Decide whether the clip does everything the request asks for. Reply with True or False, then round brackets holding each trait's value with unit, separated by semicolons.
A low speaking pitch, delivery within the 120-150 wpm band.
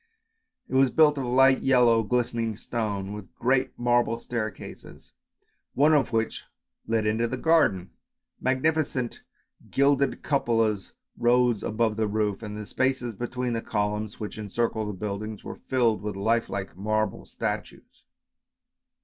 True (115 Hz; 140 wpm)